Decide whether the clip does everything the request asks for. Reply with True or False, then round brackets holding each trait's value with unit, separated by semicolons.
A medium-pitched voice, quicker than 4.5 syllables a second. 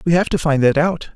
True (155 Hz; 5.7 syllables/s)